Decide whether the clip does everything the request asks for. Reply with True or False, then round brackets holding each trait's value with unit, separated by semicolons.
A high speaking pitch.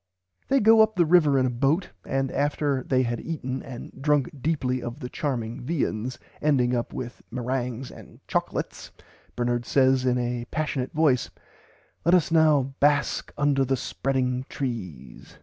False (135 Hz)